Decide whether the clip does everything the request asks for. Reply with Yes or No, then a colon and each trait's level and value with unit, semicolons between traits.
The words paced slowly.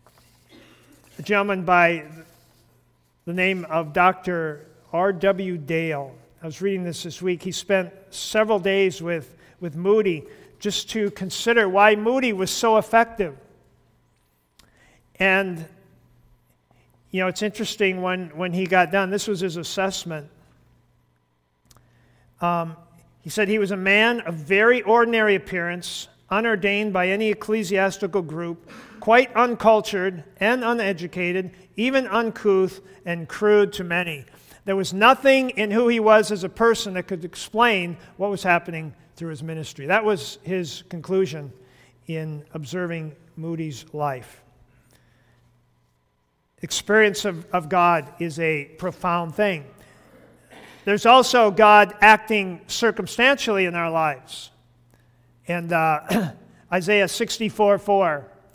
Yes: slow, 120 wpm